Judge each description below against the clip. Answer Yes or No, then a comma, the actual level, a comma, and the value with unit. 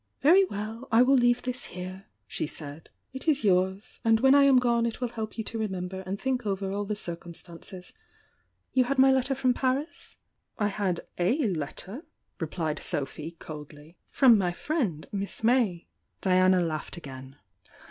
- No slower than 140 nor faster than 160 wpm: No, average, 170 wpm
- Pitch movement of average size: No, wide, 6.2 semitones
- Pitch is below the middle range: No, high, 205 Hz